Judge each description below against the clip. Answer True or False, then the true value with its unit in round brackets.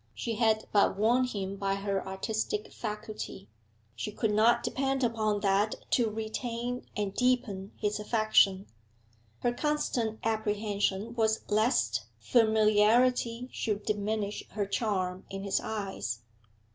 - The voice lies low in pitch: False (215 Hz)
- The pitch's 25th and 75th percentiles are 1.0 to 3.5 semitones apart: True (2.5 semitones)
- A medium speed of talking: False (120 wpm)